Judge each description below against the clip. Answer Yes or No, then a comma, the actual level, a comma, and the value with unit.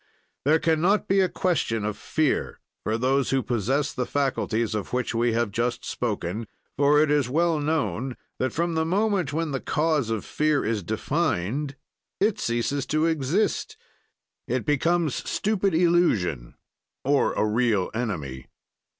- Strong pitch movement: Yes, wide, 5.8 semitones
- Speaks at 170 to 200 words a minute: No, average, 150 wpm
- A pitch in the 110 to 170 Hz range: Yes, medium, 140 Hz